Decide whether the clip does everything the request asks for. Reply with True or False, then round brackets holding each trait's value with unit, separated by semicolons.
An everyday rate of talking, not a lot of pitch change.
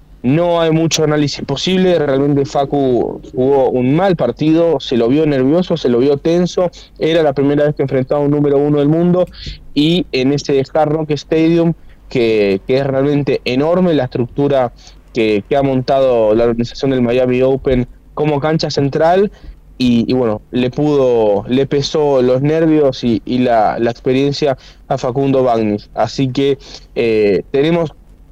False (160 wpm; 3.4 semitones)